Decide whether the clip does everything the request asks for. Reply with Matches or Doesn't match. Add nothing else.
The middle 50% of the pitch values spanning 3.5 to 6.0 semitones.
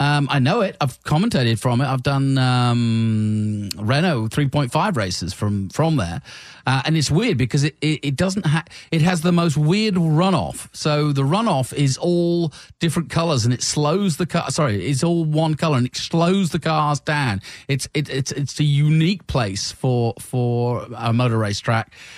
Matches